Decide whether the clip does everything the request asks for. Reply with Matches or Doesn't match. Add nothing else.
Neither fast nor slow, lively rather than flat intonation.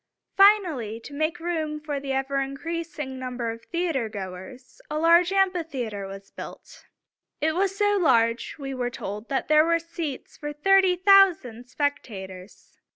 Matches